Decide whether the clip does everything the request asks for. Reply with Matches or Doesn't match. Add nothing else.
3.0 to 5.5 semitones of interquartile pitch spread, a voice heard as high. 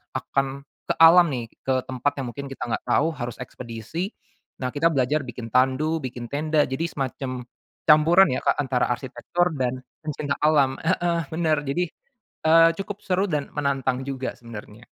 Doesn't match